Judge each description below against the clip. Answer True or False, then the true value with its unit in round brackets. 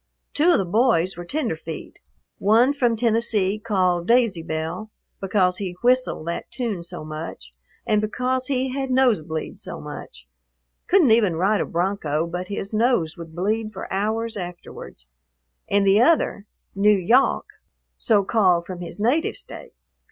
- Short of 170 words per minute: True (150 wpm)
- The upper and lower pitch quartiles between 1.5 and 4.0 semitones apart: False (5.0 semitones)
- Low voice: False (205 Hz)